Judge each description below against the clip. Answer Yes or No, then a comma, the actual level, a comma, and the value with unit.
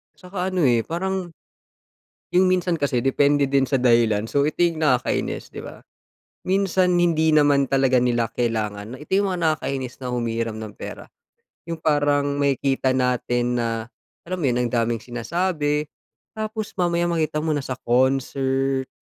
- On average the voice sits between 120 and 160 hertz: Yes, medium, 140 Hz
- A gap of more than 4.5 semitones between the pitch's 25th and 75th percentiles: Yes, wide, 5.4 semitones